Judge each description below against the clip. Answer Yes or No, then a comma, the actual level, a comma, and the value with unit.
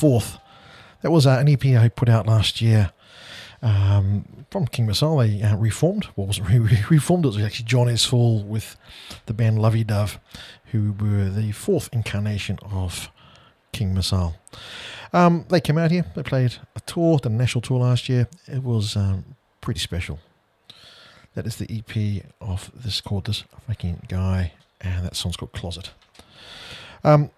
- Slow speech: No, average, 165 wpm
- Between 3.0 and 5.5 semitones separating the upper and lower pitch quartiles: Yes, average, 3.9 semitones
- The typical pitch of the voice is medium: No, low, 110 Hz